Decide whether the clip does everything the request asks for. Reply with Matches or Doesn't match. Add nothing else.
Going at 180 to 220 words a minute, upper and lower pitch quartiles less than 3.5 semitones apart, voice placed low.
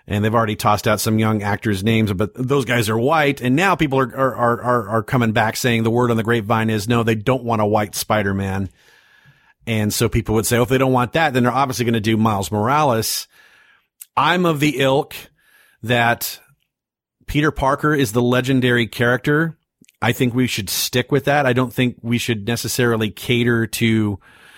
Matches